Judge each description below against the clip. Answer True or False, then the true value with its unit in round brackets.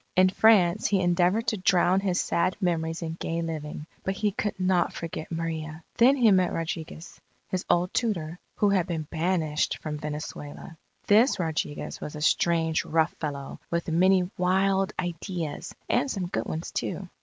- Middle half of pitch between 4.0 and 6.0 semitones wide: False (2.8 semitones)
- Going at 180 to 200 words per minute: False (165 wpm)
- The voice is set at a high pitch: False (175 Hz)